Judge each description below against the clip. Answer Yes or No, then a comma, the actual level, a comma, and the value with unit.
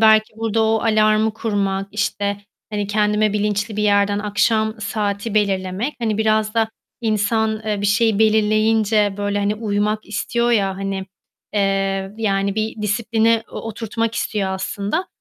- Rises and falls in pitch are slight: Yes, narrow, 1.5 semitones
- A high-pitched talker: Yes, high, 210 Hz